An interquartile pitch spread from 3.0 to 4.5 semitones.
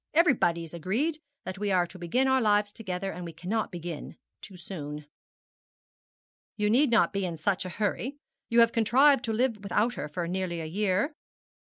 No: average, 4.9 semitones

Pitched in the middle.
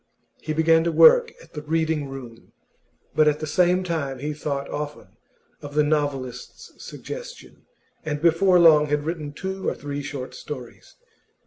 Yes: medium, 150 Hz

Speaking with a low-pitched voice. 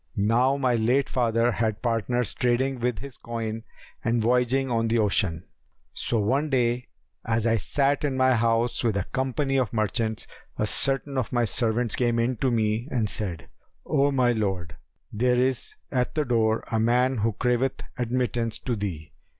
Yes: low, 120 Hz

